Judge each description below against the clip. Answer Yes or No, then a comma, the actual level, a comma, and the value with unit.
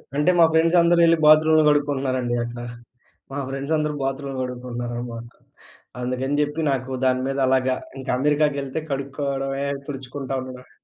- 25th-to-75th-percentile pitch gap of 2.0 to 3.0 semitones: Yes, narrow, 2.4 semitones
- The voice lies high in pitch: No, low, 135 Hz